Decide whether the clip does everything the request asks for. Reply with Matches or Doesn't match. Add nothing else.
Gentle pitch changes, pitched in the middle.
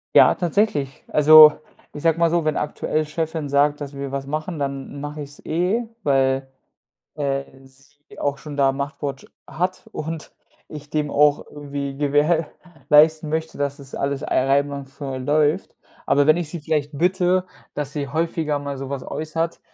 Matches